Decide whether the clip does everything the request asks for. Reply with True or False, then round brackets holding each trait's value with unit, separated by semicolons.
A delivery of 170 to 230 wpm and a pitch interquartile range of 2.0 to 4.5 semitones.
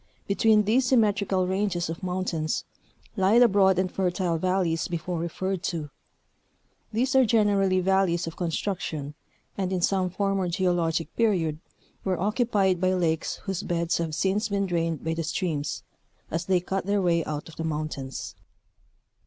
False (155 wpm; 3.0 semitones)